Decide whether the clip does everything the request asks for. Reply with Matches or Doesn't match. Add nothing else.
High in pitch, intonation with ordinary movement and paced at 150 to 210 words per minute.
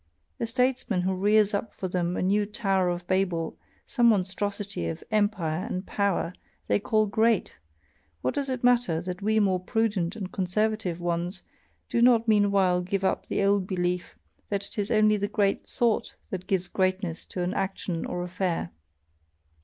Matches